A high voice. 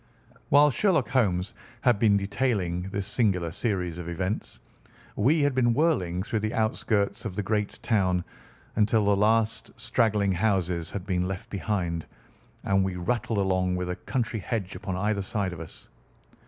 No: low, 100 Hz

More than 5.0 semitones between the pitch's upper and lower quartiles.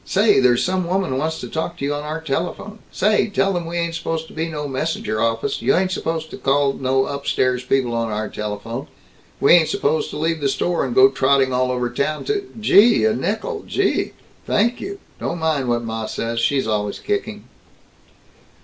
Yes: wide, 5.5 semitones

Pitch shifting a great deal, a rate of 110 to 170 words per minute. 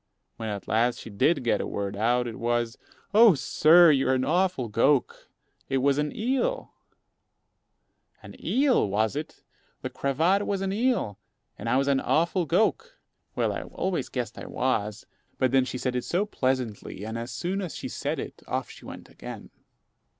No: wide, 7.5 semitones; average, 180 wpm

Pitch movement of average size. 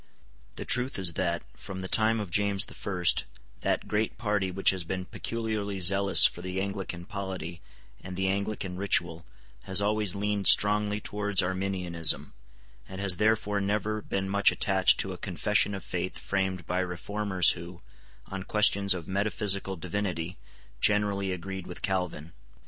No: narrow, 2.0 semitones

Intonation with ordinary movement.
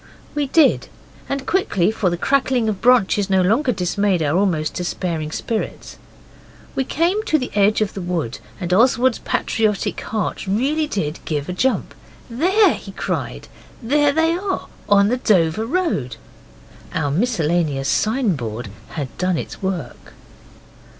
No: wide, 7.2 semitones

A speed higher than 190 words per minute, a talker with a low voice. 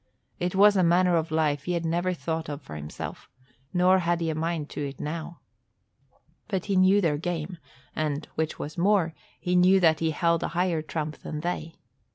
No: average, 200 wpm; medium, 170 Hz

